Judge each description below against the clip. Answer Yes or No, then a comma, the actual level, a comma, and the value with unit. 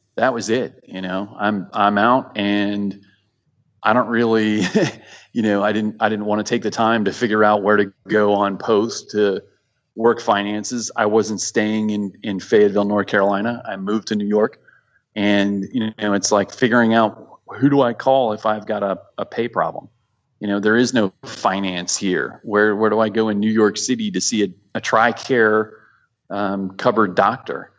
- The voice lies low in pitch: Yes, low, 105 Hz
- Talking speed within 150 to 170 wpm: No, average, 190 wpm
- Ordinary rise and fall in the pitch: No, narrow, 1.5 semitones